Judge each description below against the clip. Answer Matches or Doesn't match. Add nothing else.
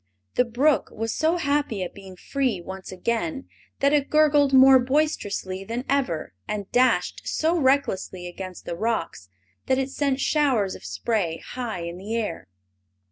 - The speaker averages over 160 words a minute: Doesn't match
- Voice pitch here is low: Doesn't match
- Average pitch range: Doesn't match